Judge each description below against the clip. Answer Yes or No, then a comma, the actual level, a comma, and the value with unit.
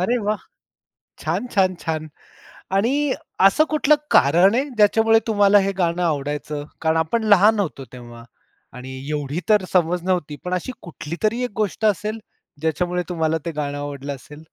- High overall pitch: No, medium, 180 Hz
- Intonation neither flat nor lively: No, wide, 5.8 semitones